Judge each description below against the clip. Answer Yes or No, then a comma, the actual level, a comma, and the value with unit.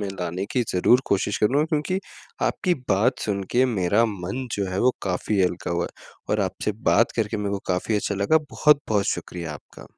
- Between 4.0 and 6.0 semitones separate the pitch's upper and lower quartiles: Yes, average, 4.9 semitones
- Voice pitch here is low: Yes, low, 105 Hz